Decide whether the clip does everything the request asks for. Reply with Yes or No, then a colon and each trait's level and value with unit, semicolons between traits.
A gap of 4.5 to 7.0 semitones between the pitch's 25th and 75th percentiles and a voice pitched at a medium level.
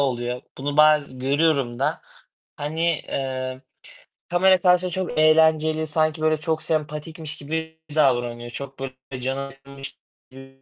No: average, 3.0 semitones; medium, 145 Hz